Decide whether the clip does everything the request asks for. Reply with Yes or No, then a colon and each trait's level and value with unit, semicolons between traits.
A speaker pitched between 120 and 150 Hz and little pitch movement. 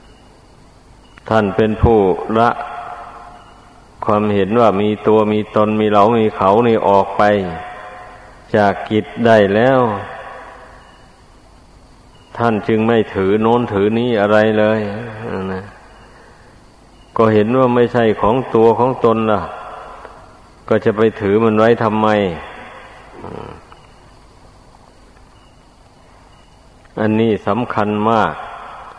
No: low, 110 Hz; narrow, 1.7 semitones